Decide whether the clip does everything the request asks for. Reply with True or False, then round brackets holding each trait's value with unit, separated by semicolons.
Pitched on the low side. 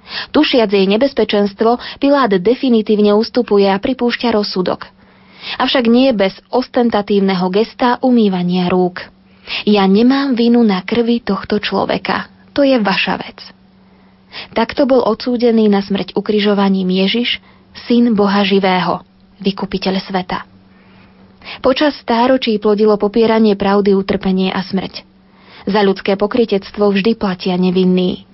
False (205 Hz)